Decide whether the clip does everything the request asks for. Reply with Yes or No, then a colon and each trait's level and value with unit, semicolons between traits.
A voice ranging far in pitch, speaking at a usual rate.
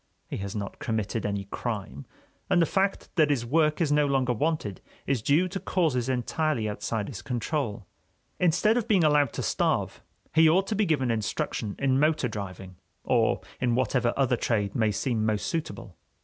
Yes: wide, 6.4 semitones; average, 175 wpm